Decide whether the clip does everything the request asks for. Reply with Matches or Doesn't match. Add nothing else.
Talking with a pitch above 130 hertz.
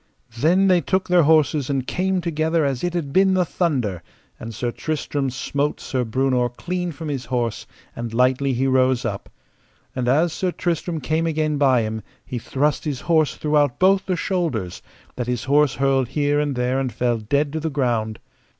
Matches